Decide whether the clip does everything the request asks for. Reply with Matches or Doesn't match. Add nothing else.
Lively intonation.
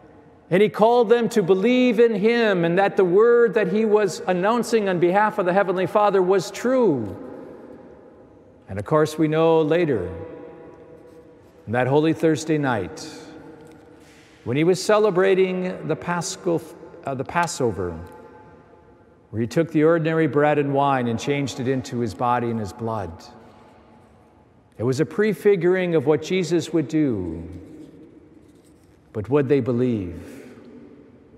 Matches